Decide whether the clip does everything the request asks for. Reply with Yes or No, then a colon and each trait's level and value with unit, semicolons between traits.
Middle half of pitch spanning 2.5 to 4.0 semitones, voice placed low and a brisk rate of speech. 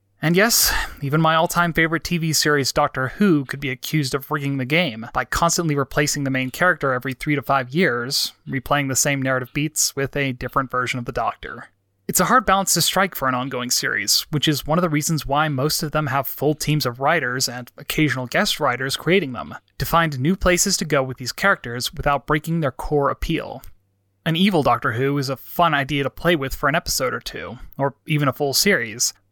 No: average, 3.6 semitones; medium, 145 Hz; fast, 220 wpm